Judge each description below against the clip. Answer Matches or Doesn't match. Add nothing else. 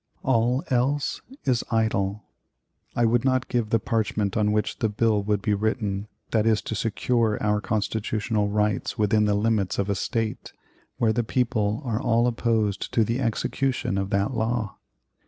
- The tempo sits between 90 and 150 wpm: Doesn't match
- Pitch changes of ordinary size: Doesn't match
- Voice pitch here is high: Doesn't match